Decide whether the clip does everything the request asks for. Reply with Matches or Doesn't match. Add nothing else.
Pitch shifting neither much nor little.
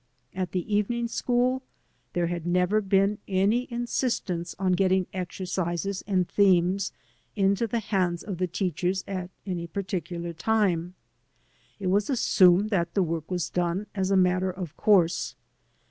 Doesn't match